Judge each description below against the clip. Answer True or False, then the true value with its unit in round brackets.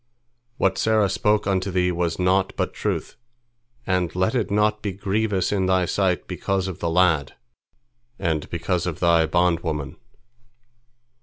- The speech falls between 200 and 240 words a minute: False (145 wpm)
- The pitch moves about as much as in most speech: False (2.3 semitones)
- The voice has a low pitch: True (90 Hz)